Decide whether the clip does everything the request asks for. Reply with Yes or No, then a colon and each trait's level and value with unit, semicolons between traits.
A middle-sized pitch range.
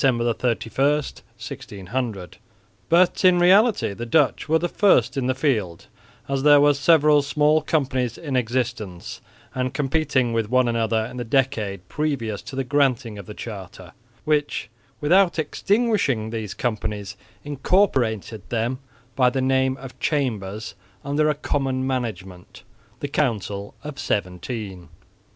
Yes: average, 4.9 semitones